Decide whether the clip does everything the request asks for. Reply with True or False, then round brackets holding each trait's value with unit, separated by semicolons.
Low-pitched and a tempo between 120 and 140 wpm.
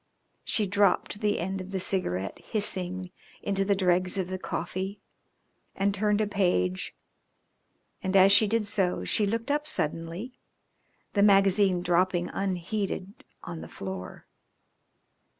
False (190 Hz; 135 wpm)